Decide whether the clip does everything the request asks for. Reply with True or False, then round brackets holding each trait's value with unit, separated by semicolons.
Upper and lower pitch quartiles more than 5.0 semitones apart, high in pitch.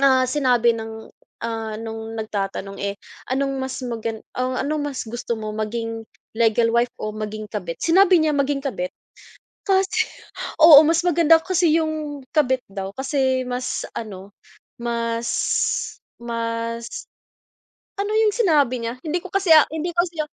True (5.5 semitones; 250 Hz)